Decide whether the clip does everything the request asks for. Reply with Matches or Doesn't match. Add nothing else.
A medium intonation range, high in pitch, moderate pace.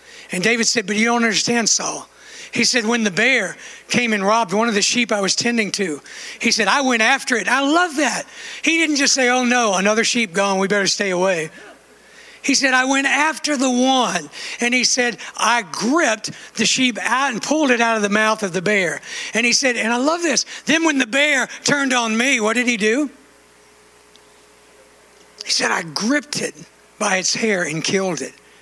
Doesn't match